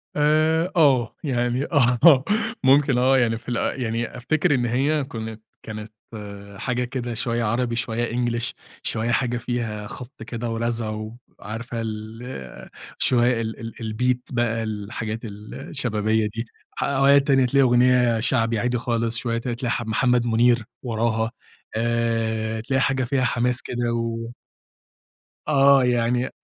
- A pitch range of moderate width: No, narrow, 2.0 semitones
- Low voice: Yes, low, 120 Hz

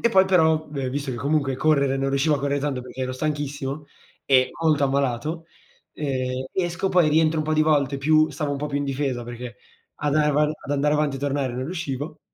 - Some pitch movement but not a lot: No, narrow, 2.3 semitones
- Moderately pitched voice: Yes, medium, 145 Hz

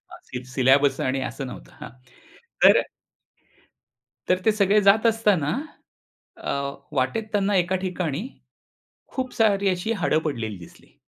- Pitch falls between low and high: Yes, medium, 180 Hz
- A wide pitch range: Yes, wide, 7.4 semitones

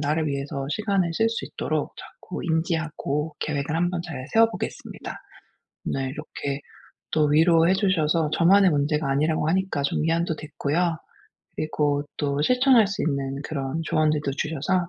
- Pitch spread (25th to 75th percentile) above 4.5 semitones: No, average, 3.3 semitones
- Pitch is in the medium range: Yes, medium, 155 Hz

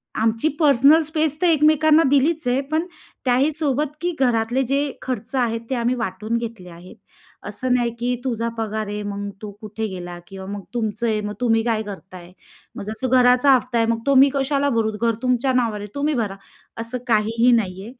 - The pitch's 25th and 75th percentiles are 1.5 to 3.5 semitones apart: No, average, 4.0 semitones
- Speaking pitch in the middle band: No, high, 235 Hz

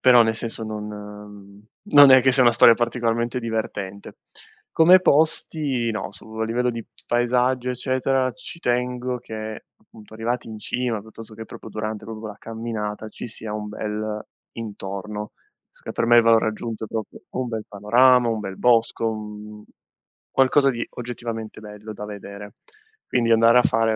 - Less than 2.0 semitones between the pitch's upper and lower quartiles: No, narrow, 2.5 semitones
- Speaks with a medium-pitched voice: No, low, 115 Hz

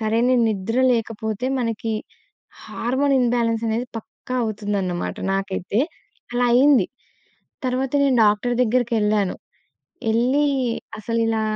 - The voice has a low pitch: No, high, 230 Hz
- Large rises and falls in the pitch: No, average, 2.7 semitones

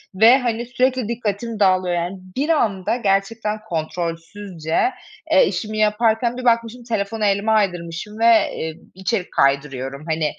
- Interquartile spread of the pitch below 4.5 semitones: No, average, 4.8 semitones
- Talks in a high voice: Yes, high, 210 Hz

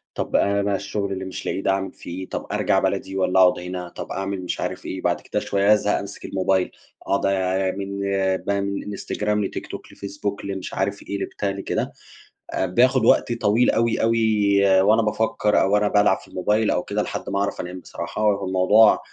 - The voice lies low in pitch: Yes, low, 100 Hz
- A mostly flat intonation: Yes, narrow, 1.6 semitones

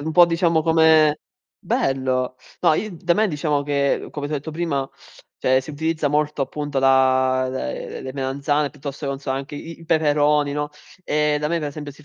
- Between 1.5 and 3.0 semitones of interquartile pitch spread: Yes, narrow, 2.6 semitones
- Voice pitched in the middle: Yes, medium, 145 Hz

